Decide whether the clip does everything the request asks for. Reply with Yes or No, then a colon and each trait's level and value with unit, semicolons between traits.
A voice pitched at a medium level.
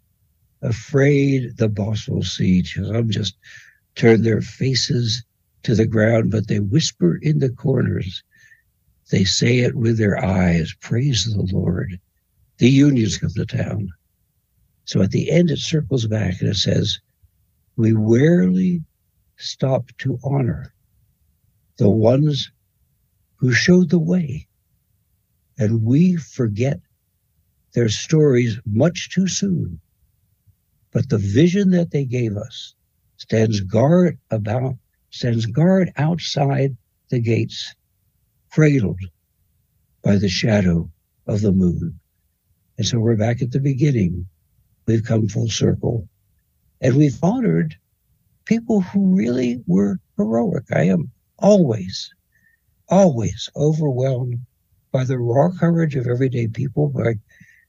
No: low, 115 Hz